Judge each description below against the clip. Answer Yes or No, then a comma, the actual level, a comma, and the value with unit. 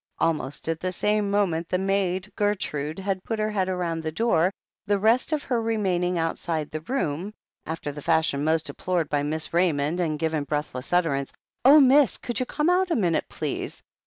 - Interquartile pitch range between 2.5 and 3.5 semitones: No, average, 4.8 semitones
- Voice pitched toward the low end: No, medium, 180 Hz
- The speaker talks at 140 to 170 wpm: No, average, 190 wpm